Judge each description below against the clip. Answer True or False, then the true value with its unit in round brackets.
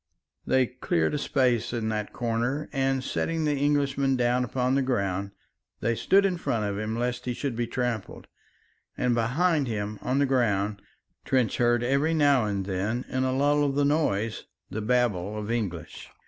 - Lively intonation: False (4.0 semitones)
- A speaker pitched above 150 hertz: False (125 Hz)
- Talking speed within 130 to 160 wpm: False (175 wpm)